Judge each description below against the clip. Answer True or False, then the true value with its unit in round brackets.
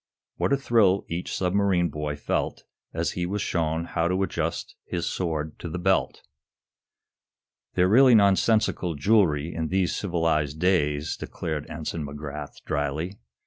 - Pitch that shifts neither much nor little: True (4.0 semitones)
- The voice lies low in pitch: True (85 Hz)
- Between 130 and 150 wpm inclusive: True (140 wpm)